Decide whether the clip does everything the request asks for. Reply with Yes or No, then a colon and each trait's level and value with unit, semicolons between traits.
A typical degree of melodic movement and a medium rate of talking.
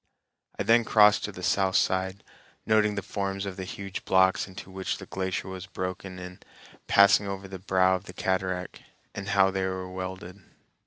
No: narrow, 0.9 semitones; average, 180 wpm